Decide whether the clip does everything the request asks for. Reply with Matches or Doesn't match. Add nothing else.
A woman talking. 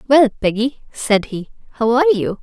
Matches